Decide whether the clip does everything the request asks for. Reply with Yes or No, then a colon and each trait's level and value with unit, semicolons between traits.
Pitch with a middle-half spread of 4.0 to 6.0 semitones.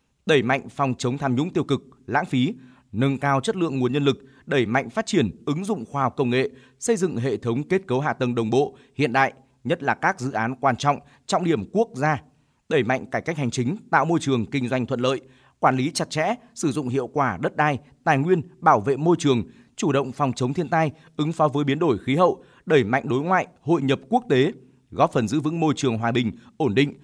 No: average, 3.3 semitones